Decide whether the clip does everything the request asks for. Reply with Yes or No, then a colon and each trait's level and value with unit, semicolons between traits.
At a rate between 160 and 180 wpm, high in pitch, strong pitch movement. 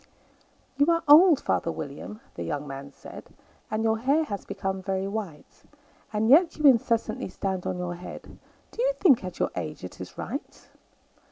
Yes: average, 175 wpm; high, 210 Hz; wide, 7.7 semitones